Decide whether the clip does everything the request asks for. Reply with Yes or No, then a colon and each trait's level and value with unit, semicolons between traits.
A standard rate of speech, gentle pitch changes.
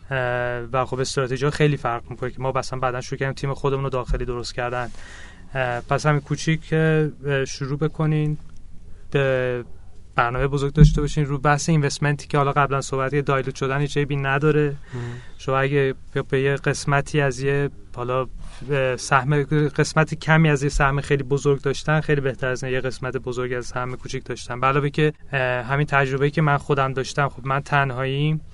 No: fast, 165 wpm; narrow, 2.2 semitones